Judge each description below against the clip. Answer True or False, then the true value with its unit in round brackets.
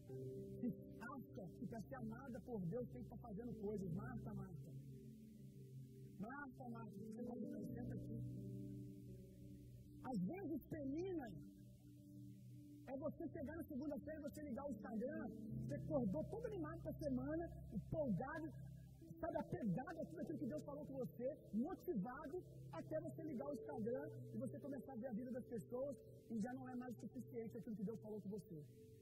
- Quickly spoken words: True (165 wpm)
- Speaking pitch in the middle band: True (165 Hz)